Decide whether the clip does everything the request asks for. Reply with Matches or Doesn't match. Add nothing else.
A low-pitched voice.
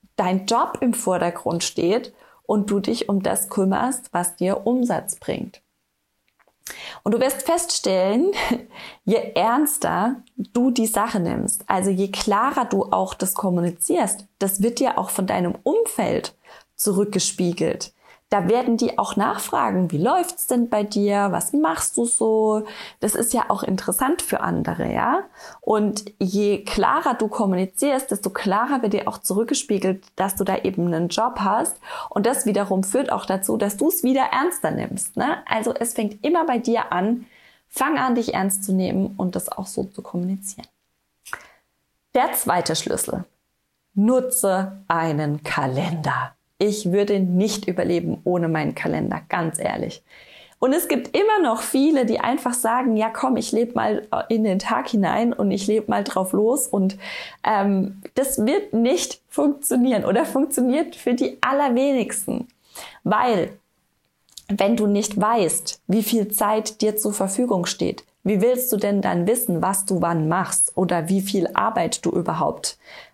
Doesn't match